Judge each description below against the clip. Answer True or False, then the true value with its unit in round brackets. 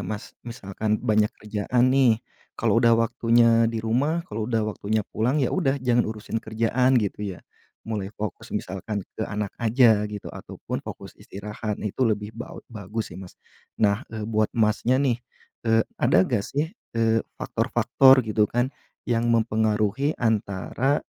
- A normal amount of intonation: False (2.2 semitones)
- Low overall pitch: True (110 Hz)